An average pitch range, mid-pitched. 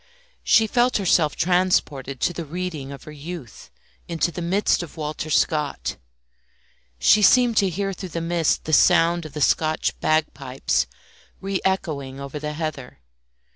Yes: average, 3.5 semitones; medium, 165 Hz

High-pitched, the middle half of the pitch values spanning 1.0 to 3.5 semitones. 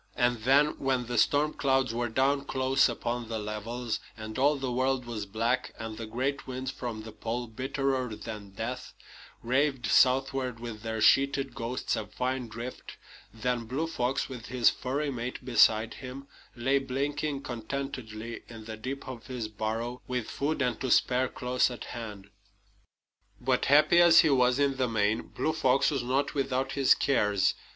No: low, 125 Hz; average, 2.8 semitones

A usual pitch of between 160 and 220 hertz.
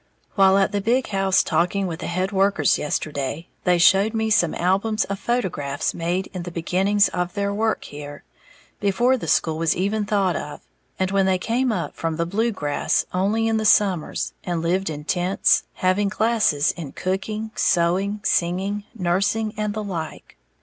Yes: high, 190 Hz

